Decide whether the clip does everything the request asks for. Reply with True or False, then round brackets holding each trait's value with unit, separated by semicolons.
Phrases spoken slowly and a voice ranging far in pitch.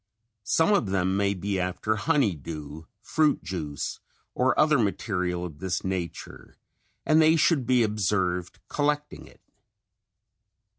True (130 wpm; 6.5 semitones)